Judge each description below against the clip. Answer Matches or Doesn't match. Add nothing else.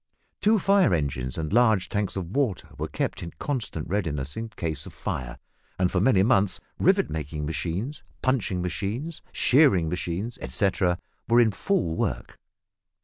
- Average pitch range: Doesn't match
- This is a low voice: Matches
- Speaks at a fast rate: Doesn't match